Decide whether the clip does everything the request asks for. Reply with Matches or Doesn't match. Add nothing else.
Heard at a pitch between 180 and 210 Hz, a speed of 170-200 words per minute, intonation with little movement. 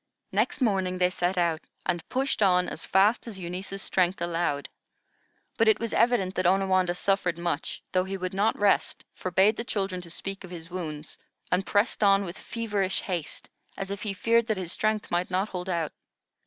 Matches